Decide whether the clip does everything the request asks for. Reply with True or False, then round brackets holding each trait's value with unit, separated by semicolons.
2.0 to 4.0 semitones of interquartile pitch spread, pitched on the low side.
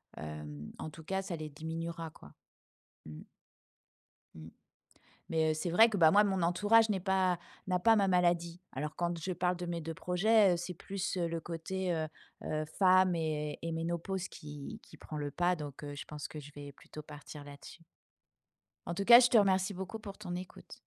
False (3.6 semitones; 170 Hz)